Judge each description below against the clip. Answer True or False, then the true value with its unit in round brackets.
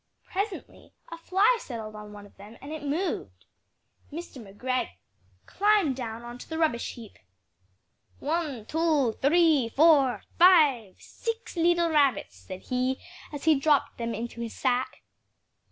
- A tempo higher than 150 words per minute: False (140 wpm)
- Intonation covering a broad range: True (6.1 semitones)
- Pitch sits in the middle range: False (280 Hz)